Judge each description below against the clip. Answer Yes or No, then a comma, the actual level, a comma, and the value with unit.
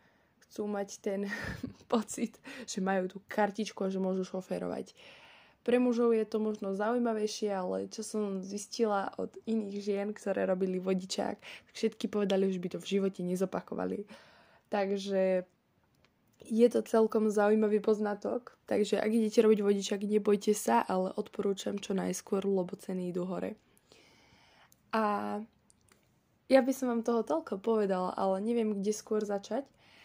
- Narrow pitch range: Yes, narrow, 2.2 semitones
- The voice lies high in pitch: Yes, high, 205 Hz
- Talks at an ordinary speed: Yes, average, 140 wpm